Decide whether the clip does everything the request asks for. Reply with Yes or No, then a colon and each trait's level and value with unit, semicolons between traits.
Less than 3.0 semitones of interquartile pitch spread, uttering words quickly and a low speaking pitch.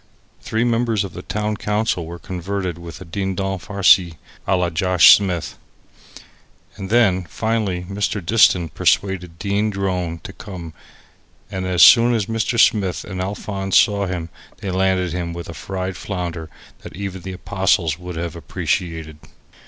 No: narrow, 2.6 semitones; average, 150 wpm; very low, 95 Hz